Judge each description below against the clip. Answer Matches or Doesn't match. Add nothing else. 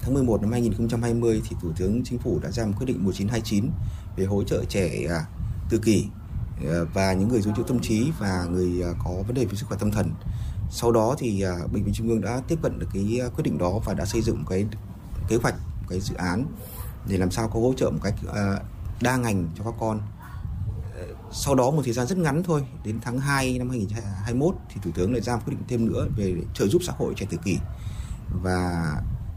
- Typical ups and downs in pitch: Matches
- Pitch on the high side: Doesn't match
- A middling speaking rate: Matches